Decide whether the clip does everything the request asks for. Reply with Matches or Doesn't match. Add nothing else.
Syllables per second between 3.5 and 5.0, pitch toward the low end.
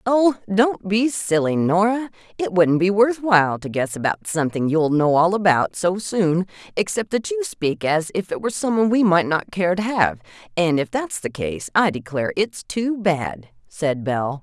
Doesn't match